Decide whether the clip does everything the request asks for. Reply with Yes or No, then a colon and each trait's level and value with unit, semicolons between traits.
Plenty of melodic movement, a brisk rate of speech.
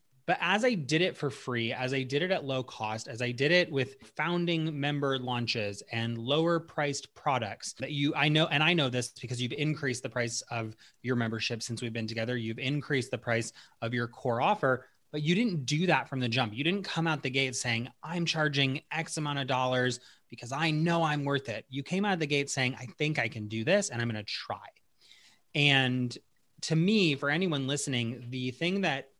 No: average, 4.1 semitones; fast, 220 wpm